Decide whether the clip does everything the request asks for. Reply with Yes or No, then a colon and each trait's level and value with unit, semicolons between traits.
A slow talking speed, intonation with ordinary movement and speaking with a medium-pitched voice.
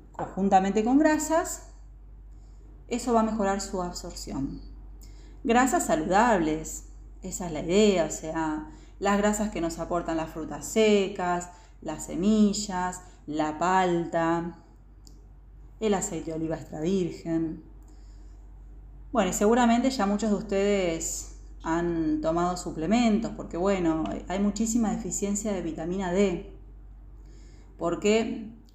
Yes: slow, 115 wpm; average, 4.4 semitones; medium, 180 Hz